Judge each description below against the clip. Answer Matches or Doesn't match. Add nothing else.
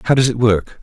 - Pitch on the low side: Matches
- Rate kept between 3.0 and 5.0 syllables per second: Doesn't match